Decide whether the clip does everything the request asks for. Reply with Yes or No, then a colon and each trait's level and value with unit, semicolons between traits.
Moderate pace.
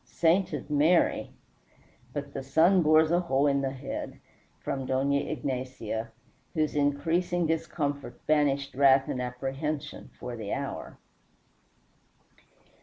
No: slow, 110 wpm